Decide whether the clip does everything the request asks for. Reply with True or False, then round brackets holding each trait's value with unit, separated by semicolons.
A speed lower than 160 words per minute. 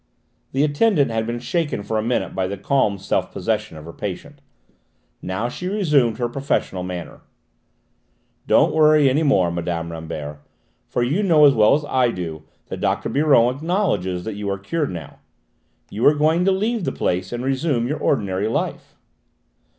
False (175 wpm)